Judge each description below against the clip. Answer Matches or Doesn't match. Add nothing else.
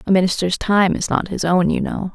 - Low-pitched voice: Doesn't match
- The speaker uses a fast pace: Matches